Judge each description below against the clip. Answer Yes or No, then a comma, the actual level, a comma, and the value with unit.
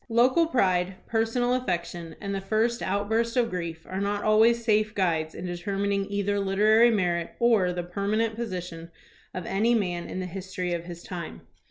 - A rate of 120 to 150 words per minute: No, average, 170 wpm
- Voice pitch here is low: No, high, 200 Hz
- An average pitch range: Yes, average, 3.9 semitones